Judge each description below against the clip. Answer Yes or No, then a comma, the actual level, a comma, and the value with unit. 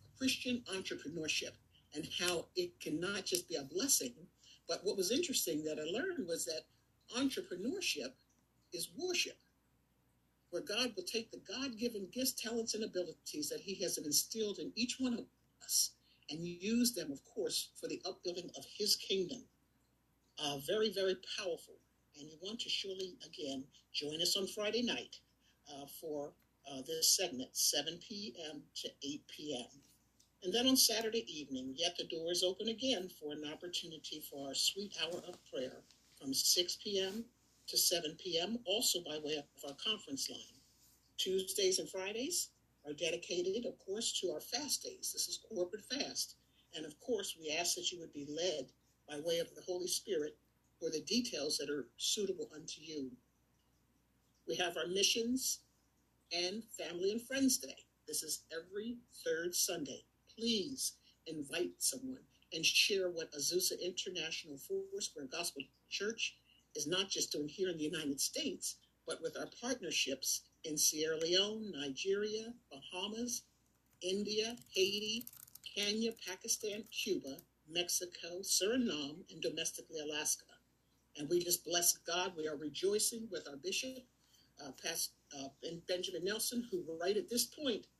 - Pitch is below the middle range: No, medium, 185 Hz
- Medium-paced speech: Yes, average, 155 wpm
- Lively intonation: Yes, wide, 7.3 semitones